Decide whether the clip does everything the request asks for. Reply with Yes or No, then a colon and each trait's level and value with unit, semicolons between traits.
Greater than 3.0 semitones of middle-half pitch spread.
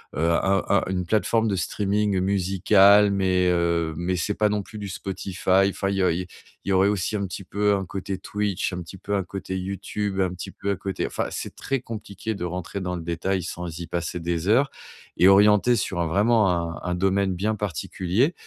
No: narrow, 2.4 semitones